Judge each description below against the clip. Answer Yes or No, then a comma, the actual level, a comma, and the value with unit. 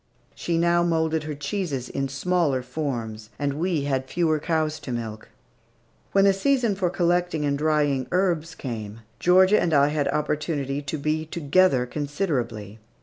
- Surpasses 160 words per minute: No, average, 150 wpm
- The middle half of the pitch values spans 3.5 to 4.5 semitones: Yes, average, 4.0 semitones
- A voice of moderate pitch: Yes, medium, 150 Hz